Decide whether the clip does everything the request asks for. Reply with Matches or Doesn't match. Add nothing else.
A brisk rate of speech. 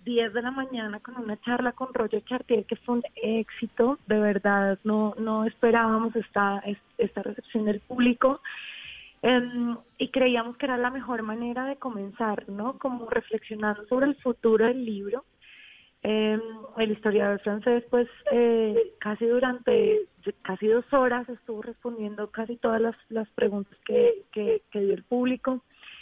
Doesn't match